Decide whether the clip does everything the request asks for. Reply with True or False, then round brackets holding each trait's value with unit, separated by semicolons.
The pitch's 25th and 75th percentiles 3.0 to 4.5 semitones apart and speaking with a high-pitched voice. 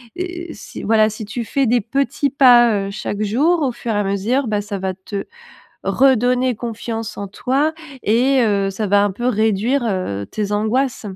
True (4.1 semitones; 225 Hz)